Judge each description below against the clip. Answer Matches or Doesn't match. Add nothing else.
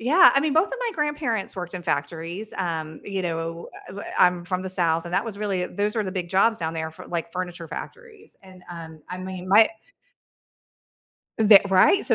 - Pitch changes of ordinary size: Matches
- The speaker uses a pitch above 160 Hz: Matches